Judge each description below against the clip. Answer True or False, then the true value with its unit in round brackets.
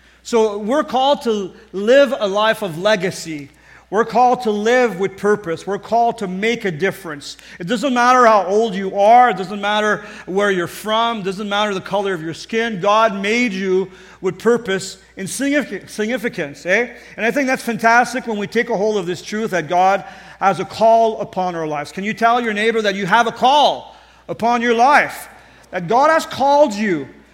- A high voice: True (210 Hz)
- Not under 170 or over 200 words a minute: True (195 wpm)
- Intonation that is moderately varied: True (3.5 semitones)